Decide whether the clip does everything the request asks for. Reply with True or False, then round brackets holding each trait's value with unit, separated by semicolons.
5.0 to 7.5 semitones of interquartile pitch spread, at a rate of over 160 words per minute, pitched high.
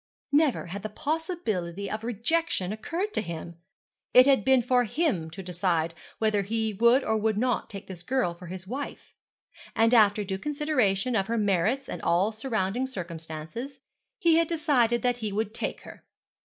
True (5.5 semitones; 170 wpm; 220 Hz)